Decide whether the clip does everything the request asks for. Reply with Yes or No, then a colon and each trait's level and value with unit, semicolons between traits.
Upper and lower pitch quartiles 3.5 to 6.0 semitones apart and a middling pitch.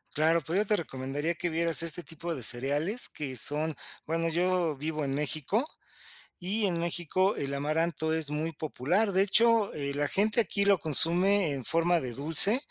Yes: average, 3.9 semitones; medium, 165 Hz